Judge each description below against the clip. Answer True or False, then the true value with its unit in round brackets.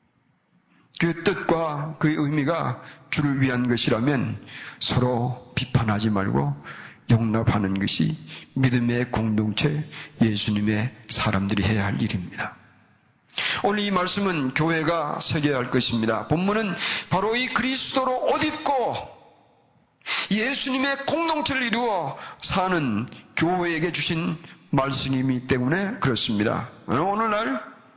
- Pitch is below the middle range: False (150 Hz)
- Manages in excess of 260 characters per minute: False (245 characters per minute)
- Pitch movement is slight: False (7.5 semitones)